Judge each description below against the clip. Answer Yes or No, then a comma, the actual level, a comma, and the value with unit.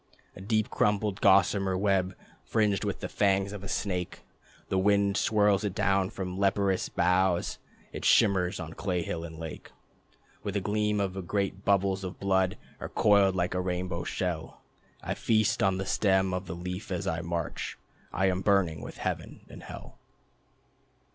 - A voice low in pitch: Yes, very low, 95 Hz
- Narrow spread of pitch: Yes, narrow, 1.7 semitones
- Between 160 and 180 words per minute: Yes, average, 170 wpm